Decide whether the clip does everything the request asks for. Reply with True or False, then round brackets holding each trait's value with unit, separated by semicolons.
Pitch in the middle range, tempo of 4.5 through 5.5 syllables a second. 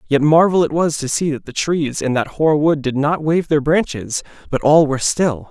True (150 Hz; 5.0 syllables/s)